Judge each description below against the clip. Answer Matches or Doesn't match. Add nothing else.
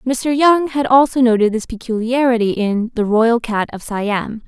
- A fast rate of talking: Doesn't match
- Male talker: Doesn't match